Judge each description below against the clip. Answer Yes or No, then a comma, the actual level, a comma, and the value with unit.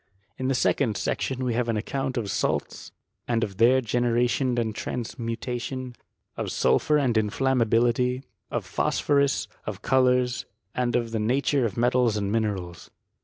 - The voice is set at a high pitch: No, low, 120 Hz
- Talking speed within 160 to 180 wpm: No, average, 150 wpm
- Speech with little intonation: Yes, narrow, 2.2 semitones